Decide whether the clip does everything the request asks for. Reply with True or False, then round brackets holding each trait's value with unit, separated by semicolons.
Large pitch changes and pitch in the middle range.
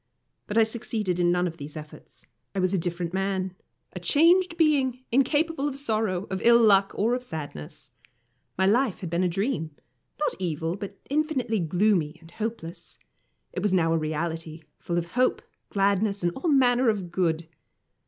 False (6.1 semitones; 195 Hz)